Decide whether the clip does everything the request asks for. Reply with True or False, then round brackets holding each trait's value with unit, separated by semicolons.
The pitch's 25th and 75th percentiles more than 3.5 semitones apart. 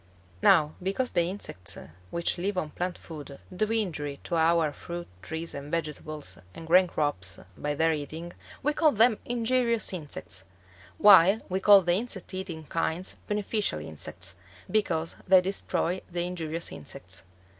True (4.1 semitones)